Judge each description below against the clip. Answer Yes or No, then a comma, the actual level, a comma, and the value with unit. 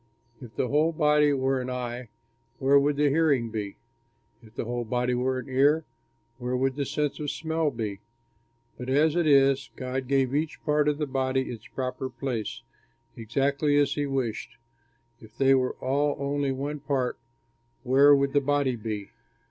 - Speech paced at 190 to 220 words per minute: No, average, 170 wpm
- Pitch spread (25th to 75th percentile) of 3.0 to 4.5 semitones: No, narrow, 2.4 semitones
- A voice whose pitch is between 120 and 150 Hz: Yes, low, 135 Hz